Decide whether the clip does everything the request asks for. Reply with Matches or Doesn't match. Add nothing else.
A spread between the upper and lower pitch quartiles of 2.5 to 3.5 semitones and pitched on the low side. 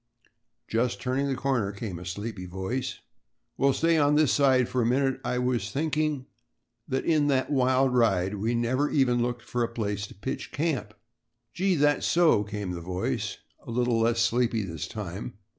Doesn't match